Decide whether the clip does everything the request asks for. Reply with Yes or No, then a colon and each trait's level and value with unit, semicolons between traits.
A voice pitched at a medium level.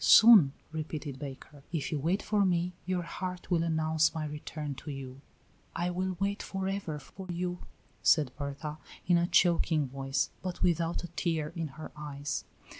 Yes: medium, 160 Hz